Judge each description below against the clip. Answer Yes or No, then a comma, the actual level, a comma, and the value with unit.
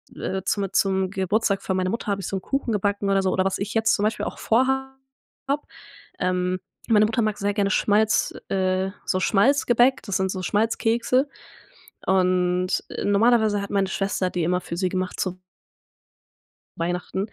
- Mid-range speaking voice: No, high, 200 Hz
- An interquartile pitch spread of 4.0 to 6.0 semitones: No, average, 2.8 semitones